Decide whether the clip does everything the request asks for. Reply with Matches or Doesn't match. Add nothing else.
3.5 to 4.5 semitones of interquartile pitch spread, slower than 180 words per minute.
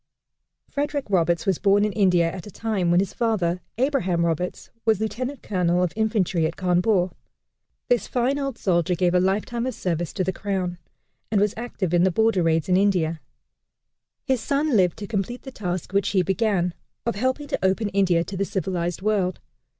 Doesn't match